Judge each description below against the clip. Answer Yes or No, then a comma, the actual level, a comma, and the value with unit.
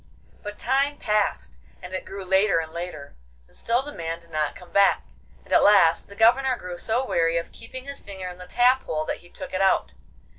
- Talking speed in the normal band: No, fast, 220 wpm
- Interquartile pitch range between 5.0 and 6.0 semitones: Yes, wide, 5.5 semitones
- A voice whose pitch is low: No, high, 190 Hz